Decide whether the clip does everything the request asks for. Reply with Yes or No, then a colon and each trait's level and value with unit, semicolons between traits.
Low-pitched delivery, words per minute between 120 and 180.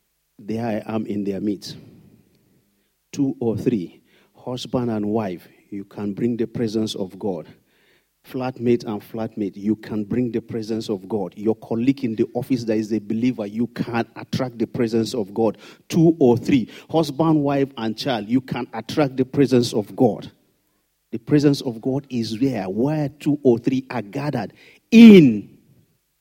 Yes: low, 120 Hz; average, 165 wpm